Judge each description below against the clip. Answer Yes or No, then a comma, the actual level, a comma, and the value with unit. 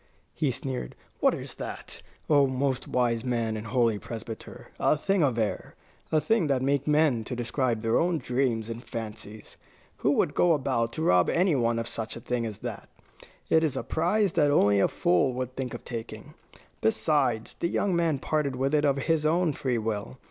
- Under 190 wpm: No, average, 195 wpm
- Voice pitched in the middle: No, low, 130 Hz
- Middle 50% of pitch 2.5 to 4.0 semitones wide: No, average, 4.8 semitones